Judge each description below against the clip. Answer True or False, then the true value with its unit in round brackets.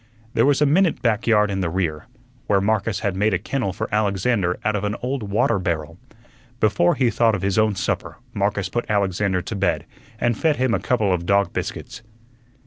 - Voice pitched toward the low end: True (105 Hz)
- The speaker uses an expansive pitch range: False (3.3 semitones)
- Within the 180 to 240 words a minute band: True (205 wpm)